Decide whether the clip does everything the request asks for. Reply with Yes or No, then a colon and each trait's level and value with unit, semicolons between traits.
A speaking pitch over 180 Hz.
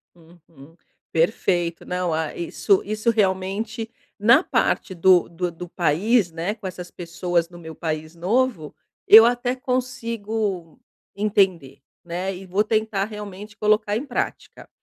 Yes: high, 190 Hz